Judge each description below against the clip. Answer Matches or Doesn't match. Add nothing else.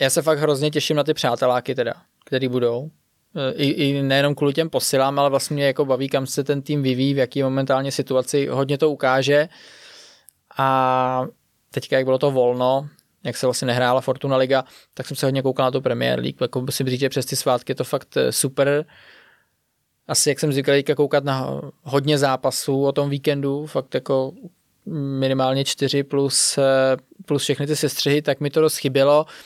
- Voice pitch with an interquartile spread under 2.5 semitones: Matches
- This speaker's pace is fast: Matches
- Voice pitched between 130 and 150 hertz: Matches